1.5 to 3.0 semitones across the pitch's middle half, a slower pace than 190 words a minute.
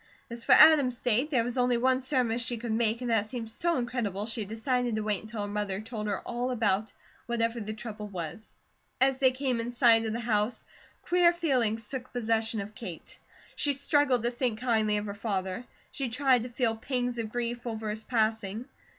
No: narrow, 2.5 semitones; average, 200 wpm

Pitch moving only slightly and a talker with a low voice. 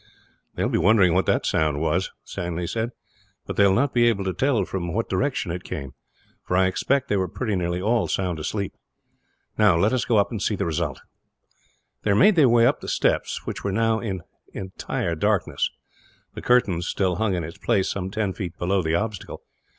No: average, 4.2 semitones; very low, 95 Hz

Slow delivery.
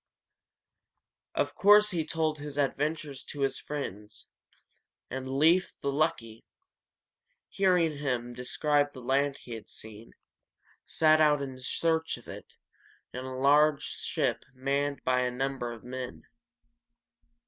Yes: slow, 125 wpm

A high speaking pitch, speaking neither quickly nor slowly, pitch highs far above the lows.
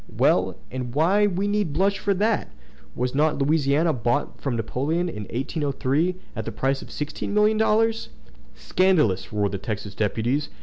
No: medium, 150 Hz; average, 160 wpm; wide, 7.4 semitones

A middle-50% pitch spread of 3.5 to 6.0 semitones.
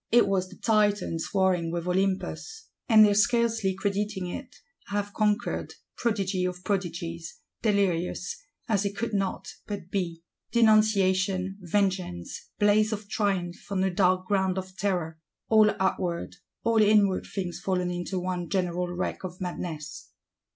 No: narrow, 2.5 semitones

